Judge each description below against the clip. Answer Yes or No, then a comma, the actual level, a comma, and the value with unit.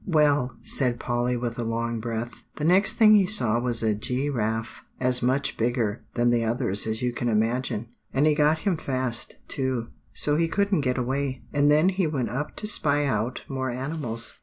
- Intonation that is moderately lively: Yes, average, 3.9 semitones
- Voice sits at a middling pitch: No, low, 125 Hz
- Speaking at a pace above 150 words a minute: Yes, average, 195 wpm